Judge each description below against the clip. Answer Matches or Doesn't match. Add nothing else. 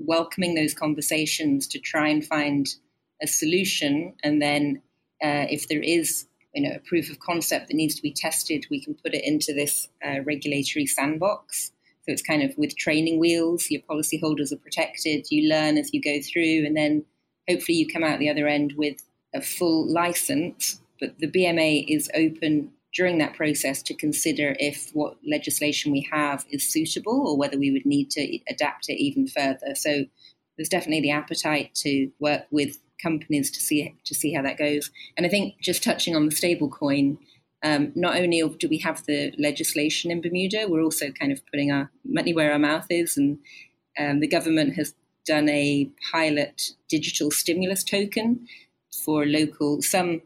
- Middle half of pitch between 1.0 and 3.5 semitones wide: Matches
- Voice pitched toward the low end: Doesn't match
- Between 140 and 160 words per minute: Doesn't match